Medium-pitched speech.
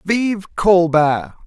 Yes: medium, 175 Hz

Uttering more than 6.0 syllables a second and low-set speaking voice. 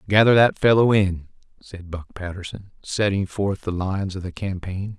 No: 4.9 syllables/s; very low, 95 Hz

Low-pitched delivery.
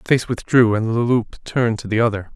Yes: low, 115 Hz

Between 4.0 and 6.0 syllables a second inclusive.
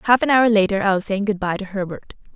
No: 6.4 syllables/s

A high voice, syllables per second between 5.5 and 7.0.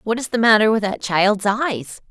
No: high, 210 Hz; 4.6 syllables/s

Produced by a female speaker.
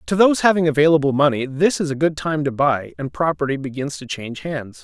No: male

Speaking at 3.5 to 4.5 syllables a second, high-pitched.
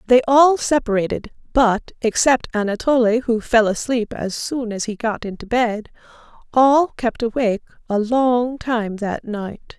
Yes: 4.2 syllables/s; high, 230 Hz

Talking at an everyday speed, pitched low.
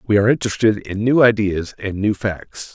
Yes: average, 195 wpm; low, 105 Hz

